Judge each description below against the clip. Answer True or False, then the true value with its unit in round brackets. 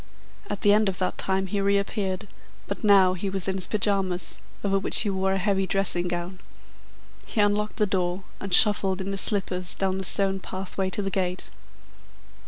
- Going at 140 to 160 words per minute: False (190 wpm)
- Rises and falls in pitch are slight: True (1.3 semitones)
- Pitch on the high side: True (195 Hz)